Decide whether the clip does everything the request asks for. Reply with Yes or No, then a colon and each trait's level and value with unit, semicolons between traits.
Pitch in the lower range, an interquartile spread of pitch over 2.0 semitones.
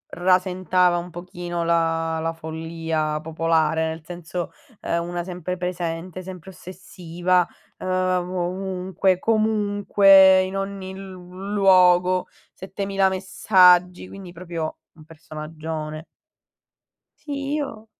No: medium, 180 Hz; narrow, 2.4 semitones